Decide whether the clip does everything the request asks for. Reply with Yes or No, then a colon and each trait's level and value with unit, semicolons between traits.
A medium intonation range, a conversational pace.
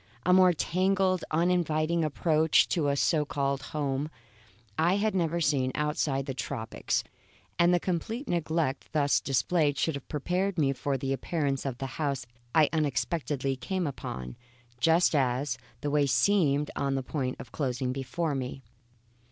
Yes: average, 4.0 semitones; average, 160 wpm